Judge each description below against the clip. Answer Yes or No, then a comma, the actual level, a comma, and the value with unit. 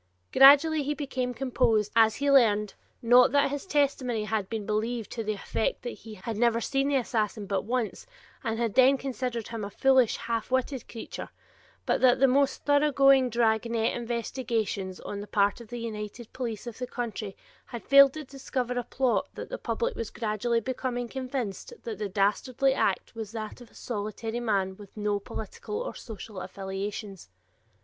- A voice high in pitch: Yes, high, 235 Hz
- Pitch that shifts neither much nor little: Yes, average, 3.6 semitones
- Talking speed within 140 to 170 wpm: No, average, 180 wpm